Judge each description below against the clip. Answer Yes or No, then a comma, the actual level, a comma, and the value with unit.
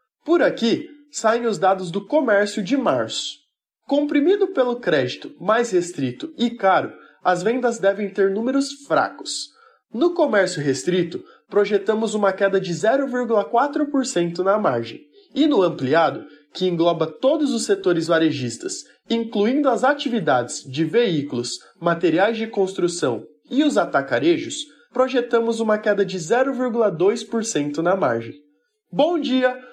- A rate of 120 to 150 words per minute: Yes, average, 125 wpm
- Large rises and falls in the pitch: Yes, wide, 6.9 semitones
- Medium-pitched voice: No, high, 225 Hz